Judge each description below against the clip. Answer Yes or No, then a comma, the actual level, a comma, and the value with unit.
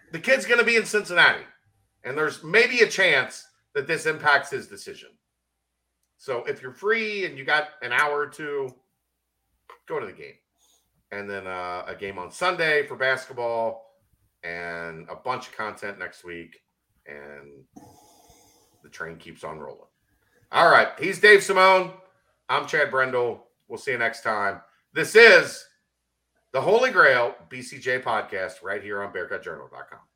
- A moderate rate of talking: Yes, average, 155 wpm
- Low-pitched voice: Yes, low, 130 Hz